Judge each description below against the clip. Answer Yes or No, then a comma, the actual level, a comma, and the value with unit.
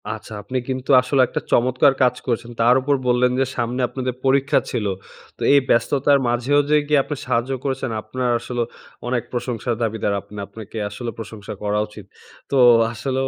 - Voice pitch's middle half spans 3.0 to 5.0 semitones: No, narrow, 2.5 semitones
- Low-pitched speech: Yes, low, 125 Hz